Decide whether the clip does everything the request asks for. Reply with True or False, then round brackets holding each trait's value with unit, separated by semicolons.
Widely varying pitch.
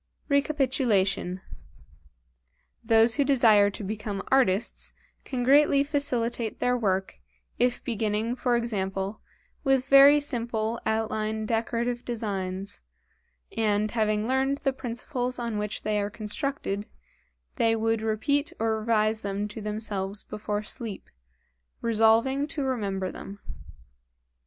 False (3.2 semitones)